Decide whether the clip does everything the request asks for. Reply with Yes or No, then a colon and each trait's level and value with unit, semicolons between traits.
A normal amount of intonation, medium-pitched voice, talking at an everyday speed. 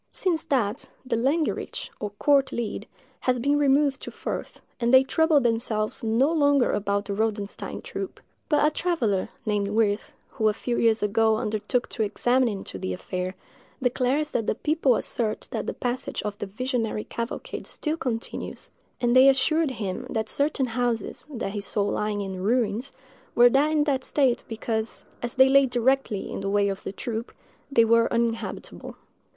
No: average, 4.2 semitones; high, 235 Hz; average, 170 wpm